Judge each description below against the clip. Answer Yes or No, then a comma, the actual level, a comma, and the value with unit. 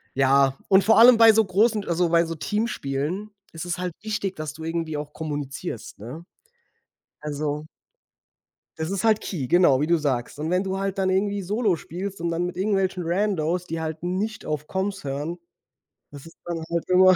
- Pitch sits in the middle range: Yes, medium, 175 Hz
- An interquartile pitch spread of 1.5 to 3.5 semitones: No, average, 4.2 semitones